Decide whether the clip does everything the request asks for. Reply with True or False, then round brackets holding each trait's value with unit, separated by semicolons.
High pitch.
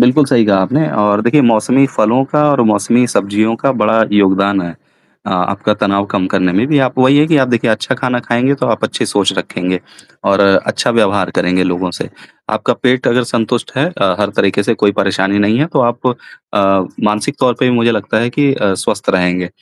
False (110 Hz)